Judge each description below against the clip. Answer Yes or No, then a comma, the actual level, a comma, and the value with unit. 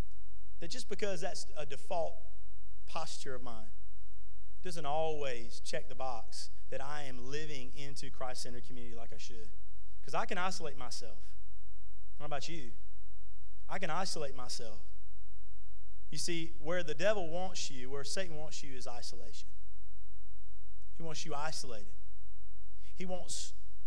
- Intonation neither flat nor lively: No, wide, 7.8 semitones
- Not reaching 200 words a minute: Yes, average, 140 wpm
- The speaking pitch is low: Yes, low, 110 Hz